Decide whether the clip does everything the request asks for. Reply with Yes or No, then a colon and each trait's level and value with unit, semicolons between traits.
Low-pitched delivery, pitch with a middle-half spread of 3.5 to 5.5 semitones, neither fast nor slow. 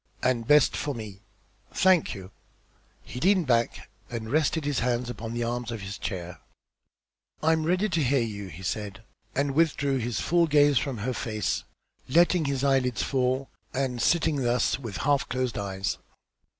Yes: low, 125 Hz; average, 4.3 semitones; average, 165 wpm